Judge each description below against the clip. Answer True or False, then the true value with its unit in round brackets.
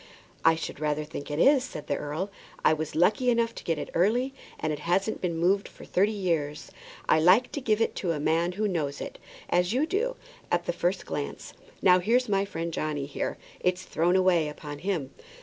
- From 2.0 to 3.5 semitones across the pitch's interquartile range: False (4.8 semitones)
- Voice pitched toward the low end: False (175 Hz)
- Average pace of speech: False (210 wpm)